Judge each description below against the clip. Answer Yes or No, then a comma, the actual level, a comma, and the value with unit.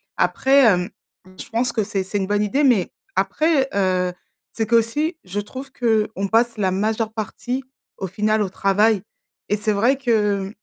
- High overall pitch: Yes, high, 215 Hz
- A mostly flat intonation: No, average, 3.2 semitones